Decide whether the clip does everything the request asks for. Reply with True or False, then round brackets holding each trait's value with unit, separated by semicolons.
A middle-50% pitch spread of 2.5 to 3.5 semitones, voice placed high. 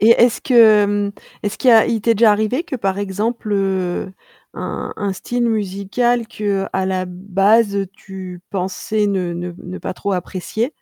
True (2.9 semitones; 200 Hz)